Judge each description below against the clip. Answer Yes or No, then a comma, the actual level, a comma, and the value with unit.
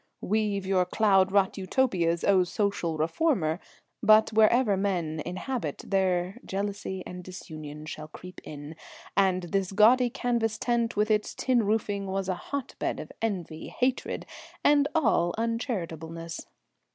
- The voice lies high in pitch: Yes, high, 195 Hz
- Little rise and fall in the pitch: No, average, 4.0 semitones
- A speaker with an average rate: No, slow, 130 wpm